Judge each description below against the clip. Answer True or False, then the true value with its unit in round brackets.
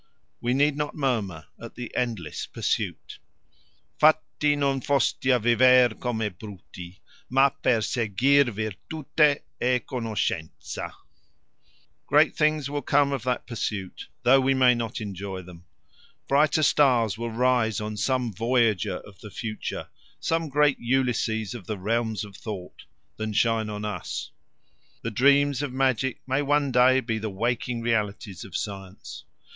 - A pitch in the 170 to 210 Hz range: False (120 Hz)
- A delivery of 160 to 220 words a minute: False (140 wpm)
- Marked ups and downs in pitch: False (4.0 semitones)